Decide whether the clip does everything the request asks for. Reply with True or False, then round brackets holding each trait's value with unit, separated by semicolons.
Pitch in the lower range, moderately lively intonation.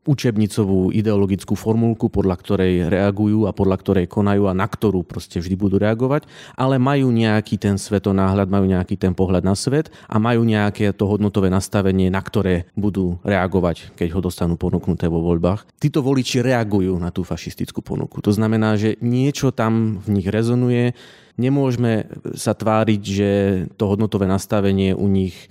True (105 Hz; 3.0 semitones)